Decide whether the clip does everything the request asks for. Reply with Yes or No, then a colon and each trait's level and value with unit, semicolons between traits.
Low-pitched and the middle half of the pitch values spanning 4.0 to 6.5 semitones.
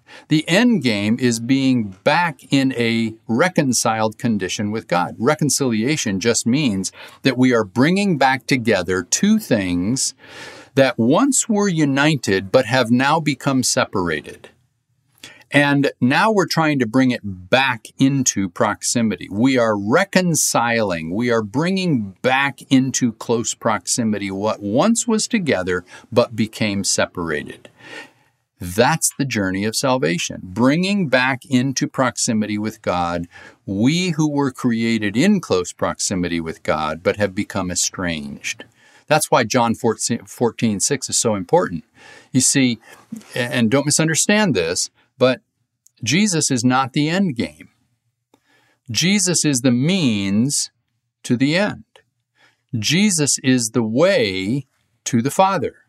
Yes: low, 125 Hz; average, 4.7 semitones